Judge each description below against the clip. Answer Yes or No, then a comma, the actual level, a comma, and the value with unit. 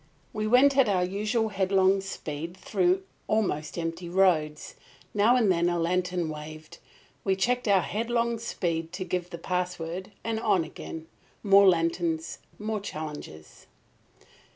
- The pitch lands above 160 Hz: Yes, medium, 185 Hz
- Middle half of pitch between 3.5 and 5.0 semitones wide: Yes, average, 4.0 semitones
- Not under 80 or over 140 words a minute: Yes, slow, 135 wpm